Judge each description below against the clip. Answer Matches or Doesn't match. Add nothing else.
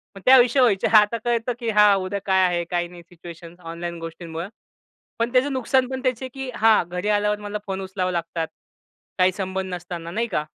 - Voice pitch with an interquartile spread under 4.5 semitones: Doesn't match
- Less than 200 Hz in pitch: Matches